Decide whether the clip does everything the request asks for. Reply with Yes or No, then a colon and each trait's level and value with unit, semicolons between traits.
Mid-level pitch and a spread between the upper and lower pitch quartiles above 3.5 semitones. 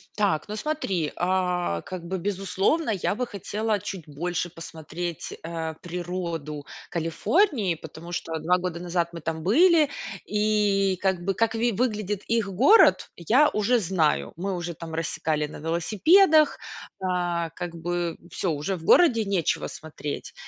Yes: medium, 180 Hz; average, 4.1 semitones